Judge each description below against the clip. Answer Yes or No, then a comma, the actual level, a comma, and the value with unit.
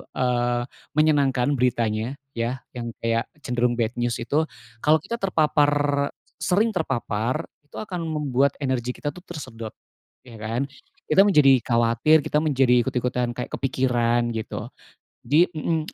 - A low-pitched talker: Yes, low, 130 Hz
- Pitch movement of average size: Yes, average, 4.1 semitones